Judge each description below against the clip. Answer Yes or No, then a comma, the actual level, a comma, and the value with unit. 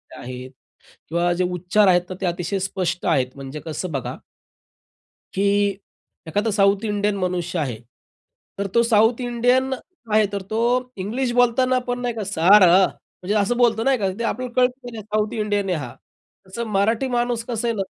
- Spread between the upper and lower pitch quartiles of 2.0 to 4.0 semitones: No, average, 4.7 semitones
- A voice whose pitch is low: No, high, 205 Hz